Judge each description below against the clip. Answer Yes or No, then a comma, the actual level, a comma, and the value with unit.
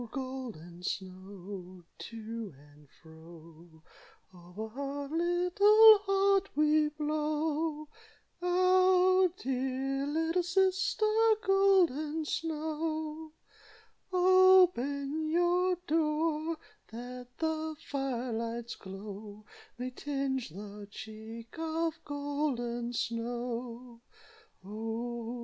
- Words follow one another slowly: Yes, slow, 80 wpm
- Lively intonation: Yes, wide, 6.1 semitones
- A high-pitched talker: Yes, very high, 280 Hz